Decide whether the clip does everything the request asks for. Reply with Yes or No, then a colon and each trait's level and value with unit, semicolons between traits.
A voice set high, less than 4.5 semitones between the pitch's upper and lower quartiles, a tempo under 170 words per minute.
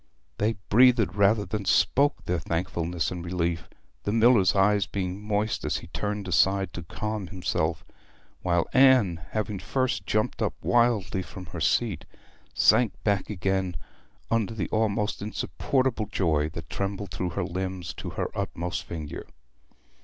No: low, 100 Hz; average, 3.5 semitones; average, 145 wpm